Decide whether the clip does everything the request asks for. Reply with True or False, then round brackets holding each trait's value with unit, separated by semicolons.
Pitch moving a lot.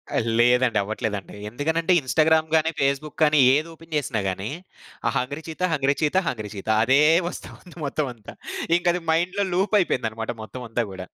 True (5.8 semitones)